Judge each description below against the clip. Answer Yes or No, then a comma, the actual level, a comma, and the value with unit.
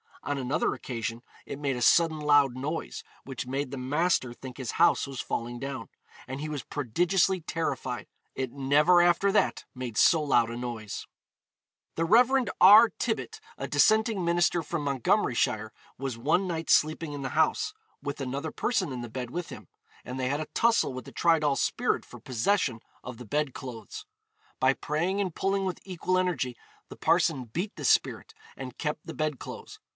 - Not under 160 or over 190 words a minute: Yes, average, 180 wpm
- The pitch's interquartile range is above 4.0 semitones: Yes, average, 5.2 semitones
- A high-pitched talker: No, medium, 145 Hz